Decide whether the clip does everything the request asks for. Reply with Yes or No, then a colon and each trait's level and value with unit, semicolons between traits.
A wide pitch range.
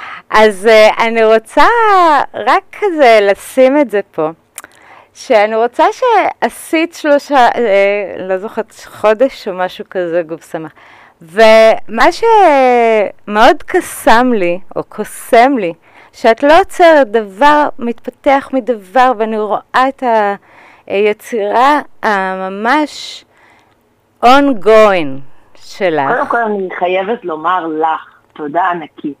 Yes: wide, 5.9 semitones